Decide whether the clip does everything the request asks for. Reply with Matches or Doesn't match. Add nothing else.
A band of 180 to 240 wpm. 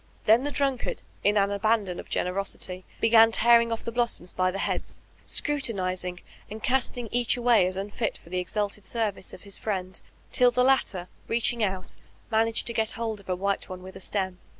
Matches